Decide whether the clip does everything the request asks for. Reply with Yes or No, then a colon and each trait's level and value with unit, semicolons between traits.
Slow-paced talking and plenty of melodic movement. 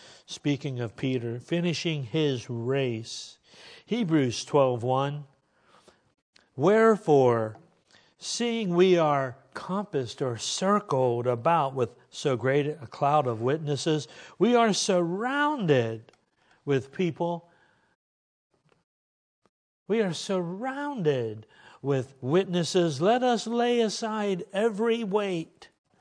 Yes: slow, 90 wpm; wide, 7.0 semitones